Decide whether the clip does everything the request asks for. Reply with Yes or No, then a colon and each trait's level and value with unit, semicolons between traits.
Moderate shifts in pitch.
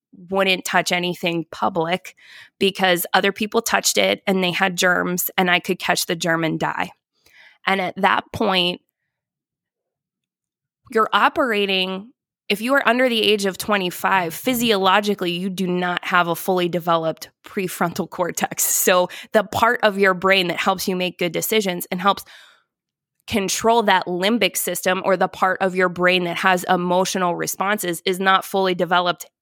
No: narrow, 2.0 semitones